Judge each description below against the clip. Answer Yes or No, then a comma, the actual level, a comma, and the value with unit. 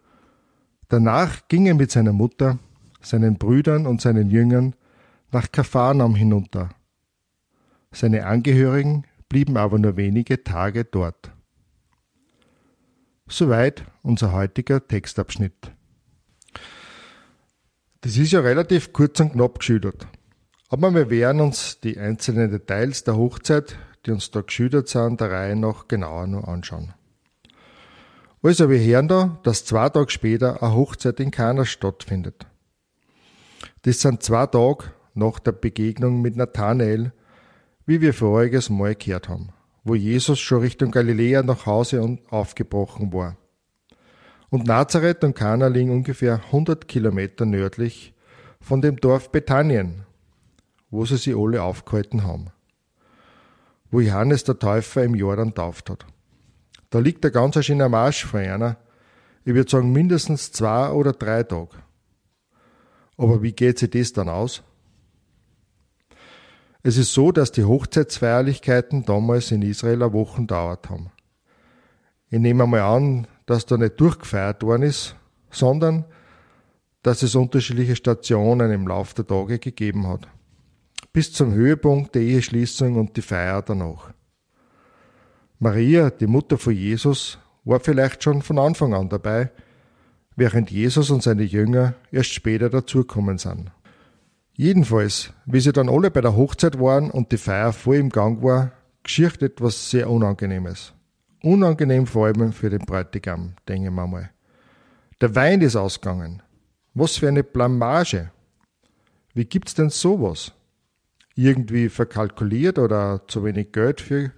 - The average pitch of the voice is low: Yes, low, 120 Hz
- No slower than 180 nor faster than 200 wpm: No, average, 135 wpm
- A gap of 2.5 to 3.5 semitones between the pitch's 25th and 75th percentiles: No, average, 4.2 semitones